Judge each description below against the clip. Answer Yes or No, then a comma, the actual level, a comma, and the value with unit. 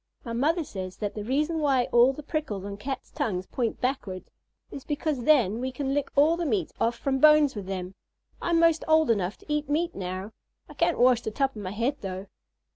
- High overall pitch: Yes, very high, 255 Hz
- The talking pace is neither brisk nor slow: No, fast, 215 wpm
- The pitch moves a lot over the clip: Yes, wide, 6.4 semitones